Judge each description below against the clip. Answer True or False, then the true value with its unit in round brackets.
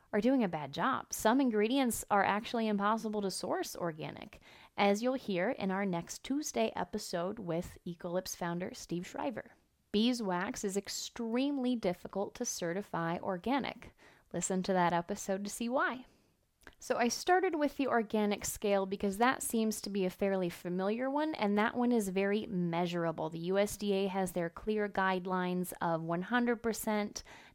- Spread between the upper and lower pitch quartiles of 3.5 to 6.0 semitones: True (4.3 semitones)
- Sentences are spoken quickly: False (150 wpm)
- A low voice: False (205 Hz)